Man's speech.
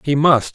Yes: male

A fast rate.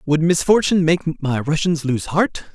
No: average, 165 wpm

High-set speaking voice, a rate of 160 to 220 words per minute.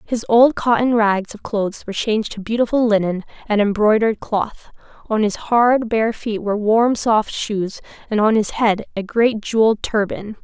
Yes: high, 220 Hz; average, 180 wpm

